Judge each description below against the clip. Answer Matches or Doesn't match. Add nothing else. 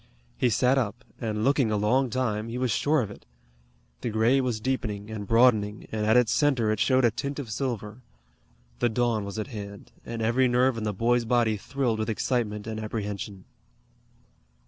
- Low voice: Matches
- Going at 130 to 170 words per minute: Doesn't match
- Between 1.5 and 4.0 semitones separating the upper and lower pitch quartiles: Matches